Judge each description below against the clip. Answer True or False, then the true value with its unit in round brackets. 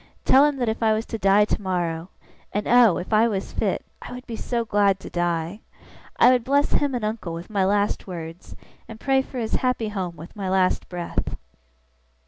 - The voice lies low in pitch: False (210 Hz)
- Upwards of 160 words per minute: True (205 wpm)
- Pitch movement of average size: True (4.3 semitones)